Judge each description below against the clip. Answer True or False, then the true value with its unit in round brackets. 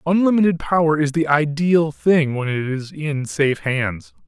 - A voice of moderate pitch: True (150 Hz)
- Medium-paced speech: True (170 wpm)